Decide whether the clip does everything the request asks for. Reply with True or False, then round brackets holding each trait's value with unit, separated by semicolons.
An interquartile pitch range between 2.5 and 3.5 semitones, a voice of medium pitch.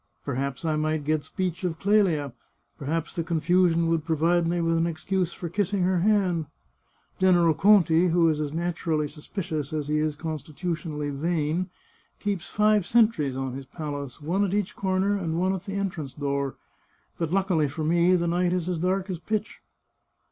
True (3.2 semitones; 170 Hz)